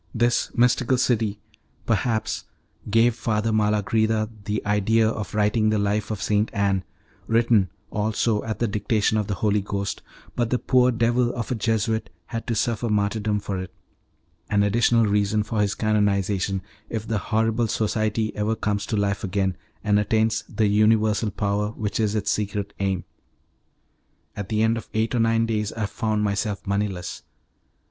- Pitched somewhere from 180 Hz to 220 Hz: No, low, 105 Hz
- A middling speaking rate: Yes, average, 160 wpm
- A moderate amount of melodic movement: No, narrow, 1.7 semitones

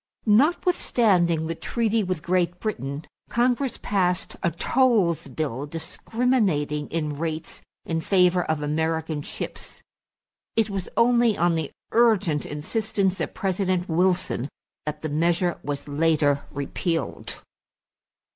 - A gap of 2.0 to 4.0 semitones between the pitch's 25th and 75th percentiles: No, average, 5.1 semitones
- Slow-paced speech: Yes, slow, 115 wpm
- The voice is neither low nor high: Yes, medium, 175 Hz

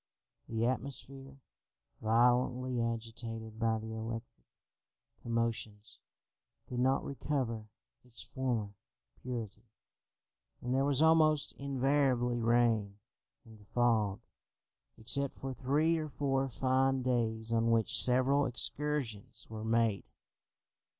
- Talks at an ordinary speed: No, slow, 100 wpm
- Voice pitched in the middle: No, low, 120 Hz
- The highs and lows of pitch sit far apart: No, average, 3.0 semitones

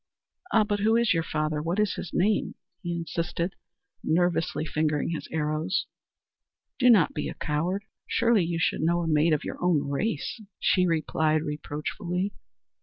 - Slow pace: No, average, 160 wpm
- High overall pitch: No, medium, 170 Hz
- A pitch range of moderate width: Yes, average, 3.9 semitones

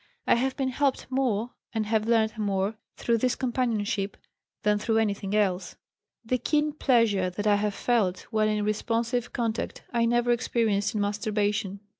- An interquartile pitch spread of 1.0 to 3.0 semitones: Yes, average, 2.7 semitones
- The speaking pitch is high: Yes, high, 220 Hz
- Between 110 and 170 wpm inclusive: Yes, average, 160 wpm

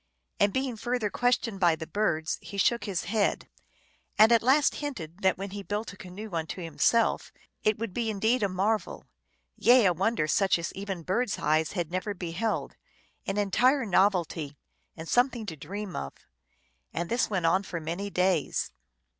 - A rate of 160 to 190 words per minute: Yes, average, 170 wpm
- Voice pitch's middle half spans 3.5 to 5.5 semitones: Yes, average, 4.3 semitones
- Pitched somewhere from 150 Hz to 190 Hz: No, high, 200 Hz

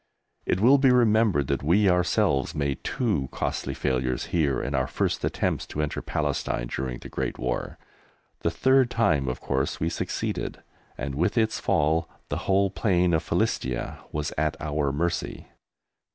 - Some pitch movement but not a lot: No, wide, 6.3 semitones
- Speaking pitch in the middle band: No, very low, 80 Hz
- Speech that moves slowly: No, average, 160 wpm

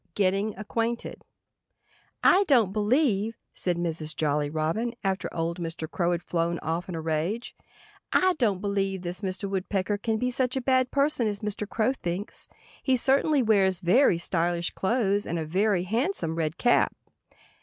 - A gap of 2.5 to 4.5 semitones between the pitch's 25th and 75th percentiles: No, average, 5.2 semitones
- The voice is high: Yes, high, 195 Hz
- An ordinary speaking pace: Yes, average, 160 wpm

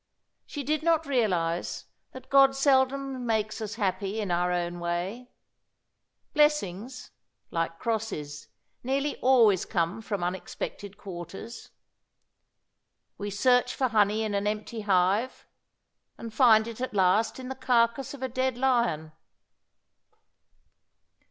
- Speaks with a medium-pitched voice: No, high, 220 Hz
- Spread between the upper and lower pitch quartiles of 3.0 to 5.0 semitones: No, wide, 5.5 semitones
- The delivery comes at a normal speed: No, slow, 120 wpm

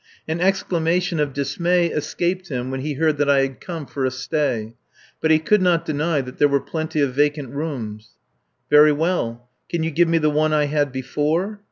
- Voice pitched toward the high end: No, medium, 150 Hz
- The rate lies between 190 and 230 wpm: Yes, average, 200 wpm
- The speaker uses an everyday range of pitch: Yes, average, 3.4 semitones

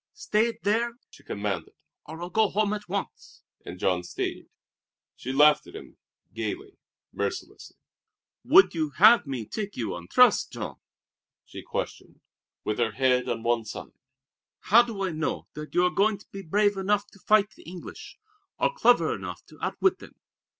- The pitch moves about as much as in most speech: No, wide, 8.6 semitones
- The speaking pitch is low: No, high, 195 Hz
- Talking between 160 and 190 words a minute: Yes, average, 170 wpm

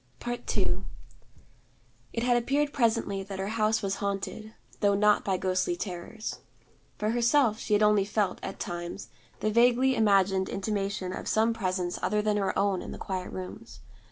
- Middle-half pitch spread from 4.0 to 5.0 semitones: No, average, 2.9 semitones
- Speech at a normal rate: Yes, average, 160 wpm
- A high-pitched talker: Yes, high, 210 Hz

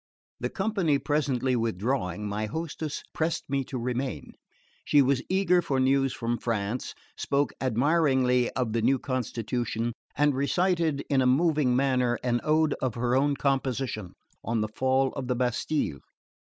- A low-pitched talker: Yes, low, 130 Hz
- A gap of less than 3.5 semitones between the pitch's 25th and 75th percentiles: Yes, average, 3.1 semitones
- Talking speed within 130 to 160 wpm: Yes, average, 150 wpm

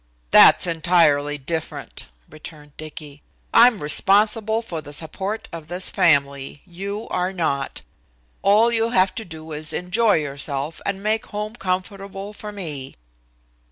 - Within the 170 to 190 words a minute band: No, slow, 135 wpm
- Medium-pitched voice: Yes, medium, 180 Hz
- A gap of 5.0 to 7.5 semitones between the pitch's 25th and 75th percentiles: Yes, average, 5.3 semitones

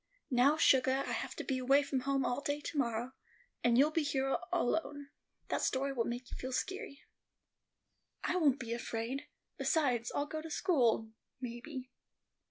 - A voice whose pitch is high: Yes, very high, 270 Hz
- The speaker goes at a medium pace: Yes, average, 170 wpm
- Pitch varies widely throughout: No, average, 2.9 semitones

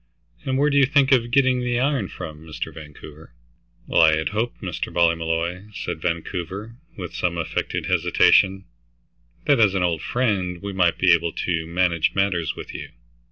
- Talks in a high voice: No, very low, 90 Hz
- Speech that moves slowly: No, average, 170 wpm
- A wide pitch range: Yes, wide, 5.8 semitones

